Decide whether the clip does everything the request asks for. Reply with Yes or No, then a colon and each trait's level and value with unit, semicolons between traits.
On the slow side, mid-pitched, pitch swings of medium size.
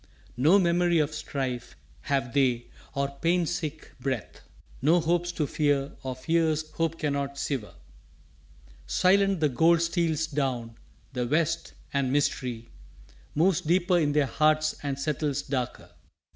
Yes: slow, 130 wpm; medium, 150 Hz; average, 3.4 semitones